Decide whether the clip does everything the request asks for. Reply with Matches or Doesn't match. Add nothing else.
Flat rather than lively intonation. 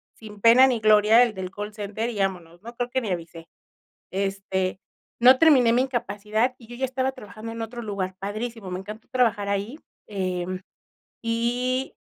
Doesn't match